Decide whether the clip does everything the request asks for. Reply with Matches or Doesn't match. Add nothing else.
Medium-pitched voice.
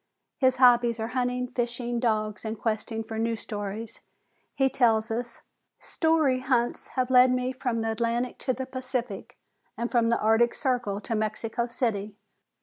Doesn't match